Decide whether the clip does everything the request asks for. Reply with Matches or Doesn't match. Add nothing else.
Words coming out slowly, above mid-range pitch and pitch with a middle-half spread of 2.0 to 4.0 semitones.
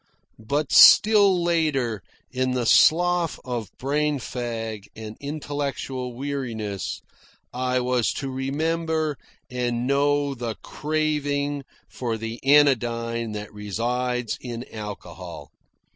Doesn't match